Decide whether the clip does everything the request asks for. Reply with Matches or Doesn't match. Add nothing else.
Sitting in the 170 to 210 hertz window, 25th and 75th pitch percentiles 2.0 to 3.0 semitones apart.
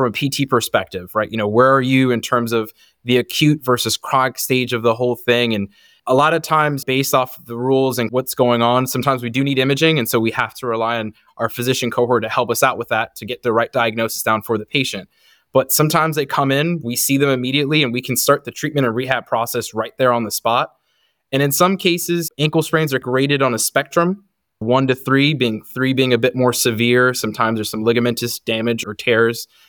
Doesn't match